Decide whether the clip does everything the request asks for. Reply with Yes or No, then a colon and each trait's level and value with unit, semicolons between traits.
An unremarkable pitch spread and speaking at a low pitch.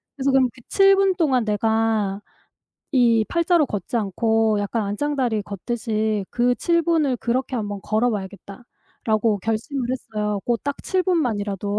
No: average, 4.2 semitones; high, 230 Hz